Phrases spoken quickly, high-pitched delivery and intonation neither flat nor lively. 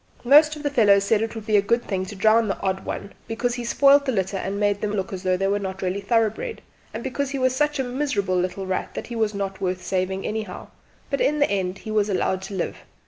Yes: fast, 260 wpm; high, 205 Hz; average, 4.2 semitones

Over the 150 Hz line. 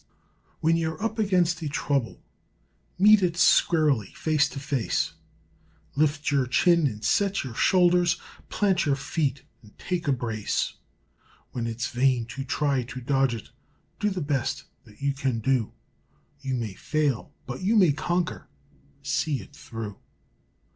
No: medium, 140 Hz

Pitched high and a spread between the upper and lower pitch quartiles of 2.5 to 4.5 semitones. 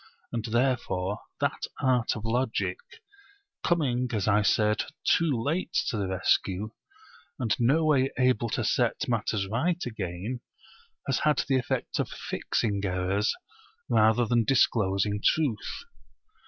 No: low, 115 Hz; average, 3.9 semitones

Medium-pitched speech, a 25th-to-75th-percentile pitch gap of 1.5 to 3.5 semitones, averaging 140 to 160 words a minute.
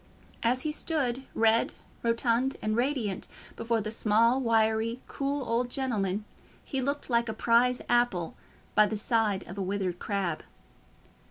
No: high, 230 Hz; average, 2.8 semitones; average, 145 wpm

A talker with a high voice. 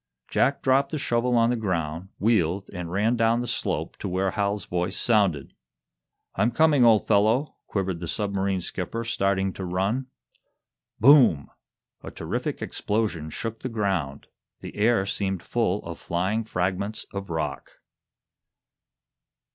No: low, 100 Hz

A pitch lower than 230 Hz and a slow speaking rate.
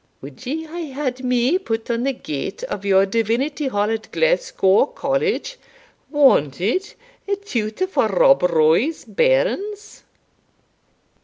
No: very high, 260 Hz; slow, 125 wpm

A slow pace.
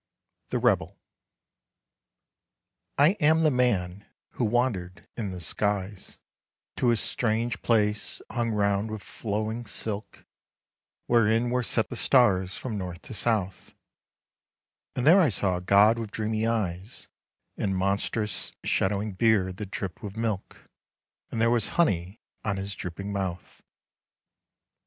Yes: slow, 130 wpm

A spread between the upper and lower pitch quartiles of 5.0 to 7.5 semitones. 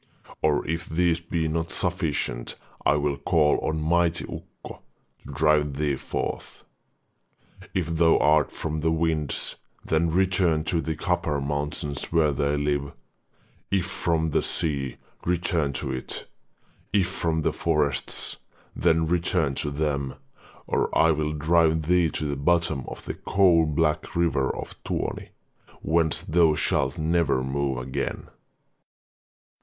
No: narrow, 2.4 semitones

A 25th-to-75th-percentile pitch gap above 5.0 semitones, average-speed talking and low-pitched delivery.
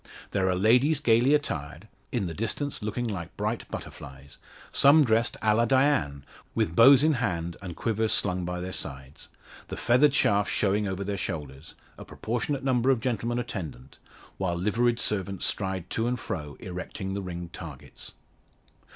Yes: wide, 5.6 semitones; average, 160 wpm; low, 105 Hz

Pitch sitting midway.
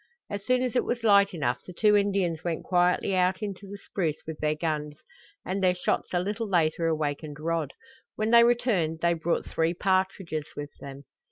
Yes: medium, 180 Hz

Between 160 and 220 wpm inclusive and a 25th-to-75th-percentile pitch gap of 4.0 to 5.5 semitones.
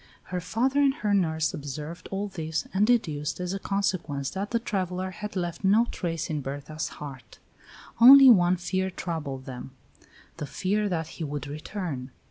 Yes: average, 165 wpm; average, 4.9 semitones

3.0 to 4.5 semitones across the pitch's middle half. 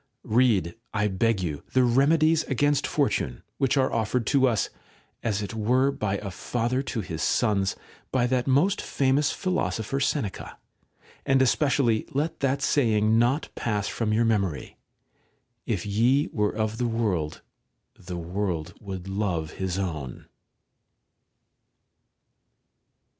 No: average, 5.1 semitones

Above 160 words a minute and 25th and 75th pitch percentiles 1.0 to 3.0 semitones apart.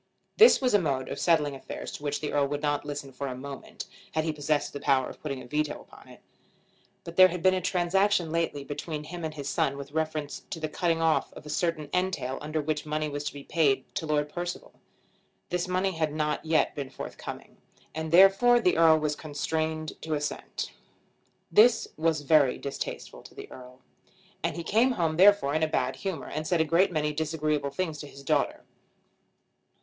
Yes: average, 200 wpm; average, 2.7 semitones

